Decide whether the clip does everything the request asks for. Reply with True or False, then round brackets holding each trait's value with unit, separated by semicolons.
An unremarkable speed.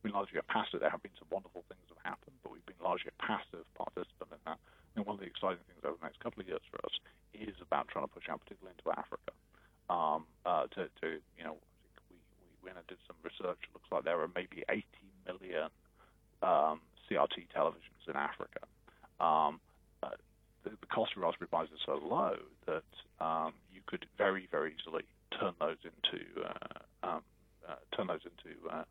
False (215 wpm)